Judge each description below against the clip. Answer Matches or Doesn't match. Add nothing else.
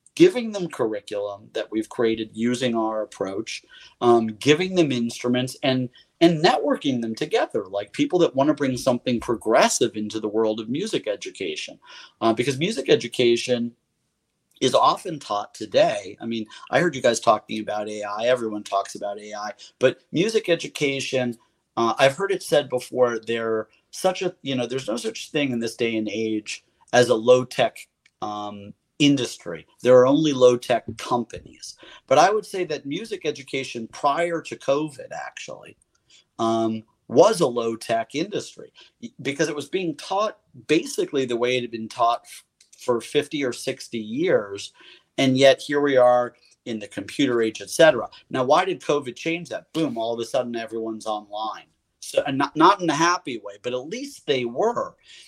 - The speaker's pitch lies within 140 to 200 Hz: Doesn't match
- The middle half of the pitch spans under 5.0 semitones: Doesn't match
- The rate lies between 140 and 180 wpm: Matches